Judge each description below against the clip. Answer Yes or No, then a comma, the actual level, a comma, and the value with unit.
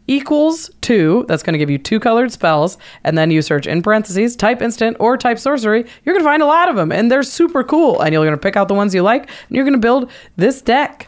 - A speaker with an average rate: No, fast, 270 wpm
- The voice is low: No, high, 235 Hz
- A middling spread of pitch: No, wide, 6.9 semitones